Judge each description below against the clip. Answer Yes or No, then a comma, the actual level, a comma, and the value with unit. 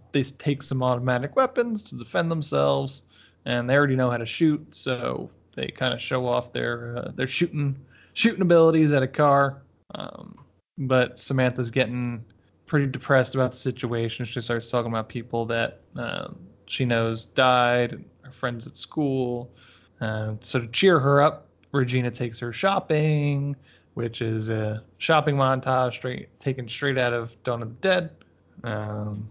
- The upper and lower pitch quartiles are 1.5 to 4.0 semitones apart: Yes, average, 3.3 semitones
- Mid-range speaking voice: No, low, 125 Hz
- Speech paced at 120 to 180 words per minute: Yes, average, 160 wpm